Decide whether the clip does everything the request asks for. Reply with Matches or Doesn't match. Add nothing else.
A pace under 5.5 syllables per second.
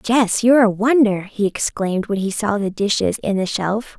Matches